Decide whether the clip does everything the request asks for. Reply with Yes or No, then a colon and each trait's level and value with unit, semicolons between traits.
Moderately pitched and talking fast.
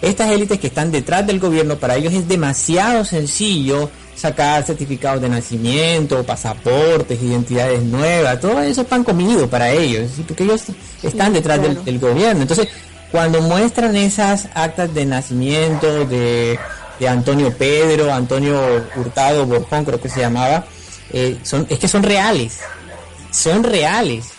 No: medium, 145 Hz; average, 145 wpm